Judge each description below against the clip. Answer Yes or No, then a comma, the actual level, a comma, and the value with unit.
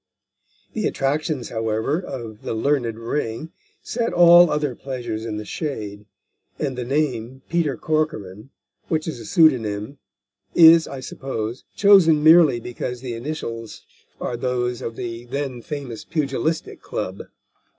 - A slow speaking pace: Yes, slow, 130 wpm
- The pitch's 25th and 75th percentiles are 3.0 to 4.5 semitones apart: No, average, 5.1 semitones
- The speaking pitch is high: No, low, 130 Hz